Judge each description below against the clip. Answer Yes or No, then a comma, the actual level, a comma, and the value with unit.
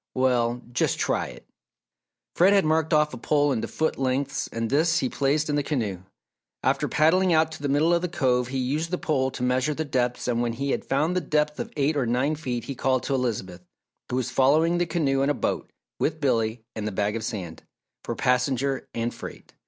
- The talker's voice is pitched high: No, low, 135 Hz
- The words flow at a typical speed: No, fast, 220 wpm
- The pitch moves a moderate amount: Yes, average, 3.8 semitones